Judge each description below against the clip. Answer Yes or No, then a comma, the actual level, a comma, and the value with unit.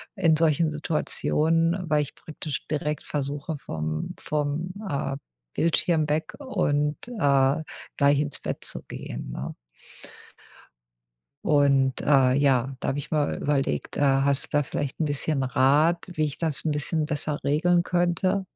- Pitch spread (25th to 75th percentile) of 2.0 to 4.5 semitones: Yes, narrow, 2.6 semitones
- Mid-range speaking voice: Yes, medium, 150 Hz